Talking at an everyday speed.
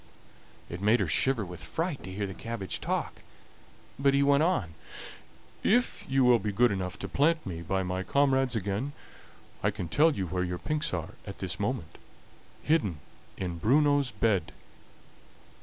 Yes: average, 165 wpm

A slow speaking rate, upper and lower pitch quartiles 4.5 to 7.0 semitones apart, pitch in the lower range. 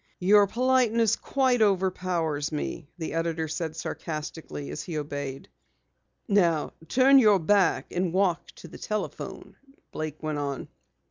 No: slow, 130 wpm; average, 5.0 semitones; medium, 170 Hz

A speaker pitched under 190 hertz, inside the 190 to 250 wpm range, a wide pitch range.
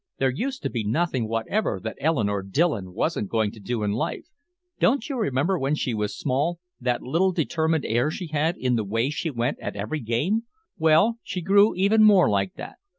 Yes: medium, 140 Hz; average, 200 wpm; wide, 7.5 semitones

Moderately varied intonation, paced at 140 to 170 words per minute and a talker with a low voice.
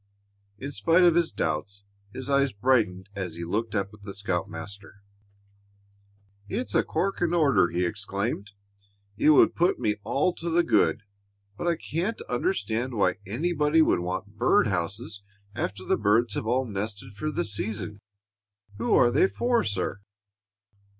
No: wide, 6.6 semitones; average, 150 wpm; low, 110 Hz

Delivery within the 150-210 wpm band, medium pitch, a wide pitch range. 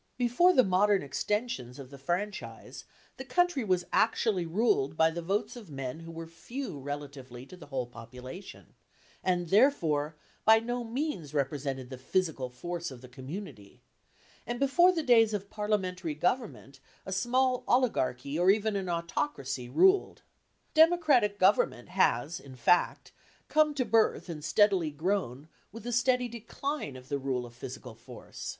Yes: average, 155 wpm; medium, 180 Hz; wide, 8.9 semitones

